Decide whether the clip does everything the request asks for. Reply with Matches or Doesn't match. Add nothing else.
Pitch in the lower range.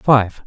Matches